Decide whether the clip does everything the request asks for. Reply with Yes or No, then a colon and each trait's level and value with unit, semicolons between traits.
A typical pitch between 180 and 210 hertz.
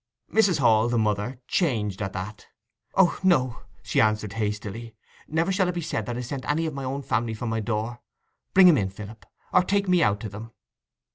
No: low, 120 Hz